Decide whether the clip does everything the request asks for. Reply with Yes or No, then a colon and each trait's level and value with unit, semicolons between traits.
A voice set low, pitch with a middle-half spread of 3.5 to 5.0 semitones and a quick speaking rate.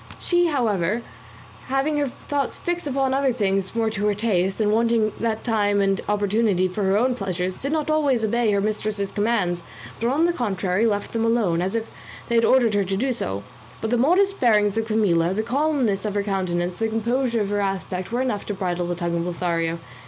No: high, 215 Hz; average, 3.9 semitones; fast, 210 wpm